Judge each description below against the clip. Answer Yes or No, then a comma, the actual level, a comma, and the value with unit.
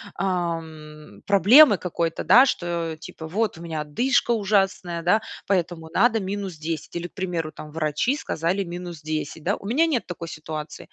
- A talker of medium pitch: Yes, medium, 175 Hz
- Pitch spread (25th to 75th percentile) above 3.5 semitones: Yes, average, 3.9 semitones